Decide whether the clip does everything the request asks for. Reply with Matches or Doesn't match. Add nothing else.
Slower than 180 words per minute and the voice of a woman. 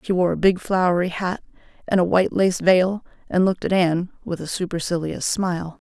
Doesn't match